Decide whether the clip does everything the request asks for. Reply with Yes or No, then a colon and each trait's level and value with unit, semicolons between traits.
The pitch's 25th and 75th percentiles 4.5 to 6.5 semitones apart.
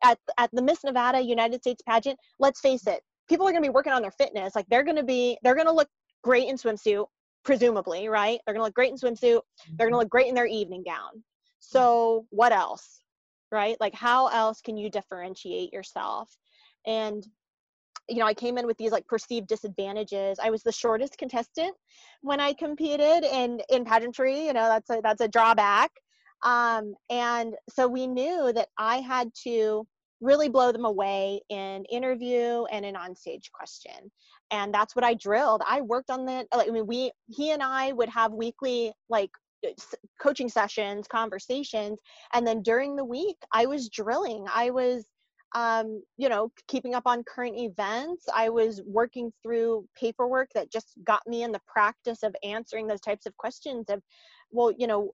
No: average, 2.8 semitones